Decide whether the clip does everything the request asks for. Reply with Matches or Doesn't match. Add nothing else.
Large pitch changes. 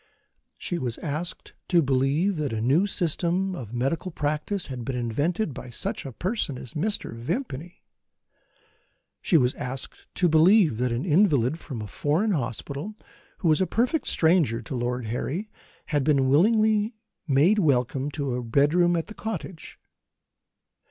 Matches